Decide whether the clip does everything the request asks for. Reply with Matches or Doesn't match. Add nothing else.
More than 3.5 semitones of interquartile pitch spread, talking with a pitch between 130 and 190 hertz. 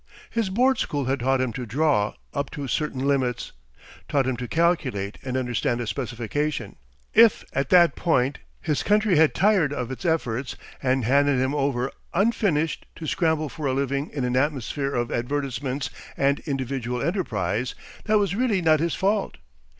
Matches